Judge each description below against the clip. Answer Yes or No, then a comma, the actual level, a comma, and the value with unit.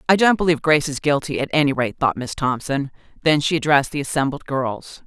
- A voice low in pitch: No, medium, 145 Hz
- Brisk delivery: Yes, fast, 215 wpm